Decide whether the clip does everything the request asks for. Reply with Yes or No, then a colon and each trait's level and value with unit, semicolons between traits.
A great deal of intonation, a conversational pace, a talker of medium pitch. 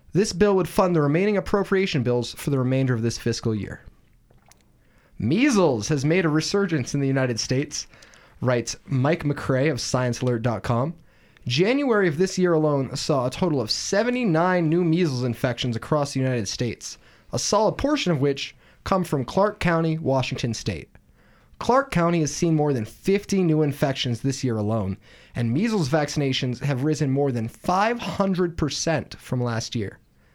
Yes: wide, 6.0 semitones; average, 160 wpm; medium, 145 Hz